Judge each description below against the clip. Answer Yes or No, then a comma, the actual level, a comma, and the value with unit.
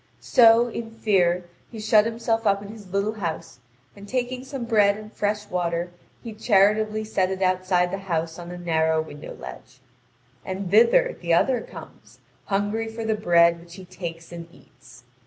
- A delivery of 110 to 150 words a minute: No, average, 175 wpm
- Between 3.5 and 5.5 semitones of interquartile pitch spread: Yes, average, 4.1 semitones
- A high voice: Yes, high, 200 Hz